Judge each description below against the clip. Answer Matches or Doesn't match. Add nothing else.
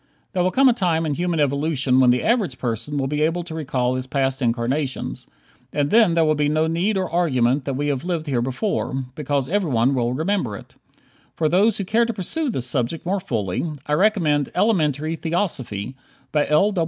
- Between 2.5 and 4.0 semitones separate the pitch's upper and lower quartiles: Doesn't match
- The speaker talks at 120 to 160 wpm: Doesn't match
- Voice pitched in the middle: Matches